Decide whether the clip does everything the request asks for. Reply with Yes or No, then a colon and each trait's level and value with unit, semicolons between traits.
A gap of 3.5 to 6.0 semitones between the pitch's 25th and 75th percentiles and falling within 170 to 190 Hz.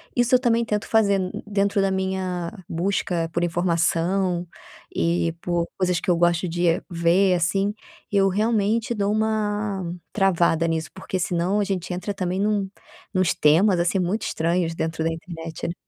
No: average, 2.8 semitones; medium, 185 Hz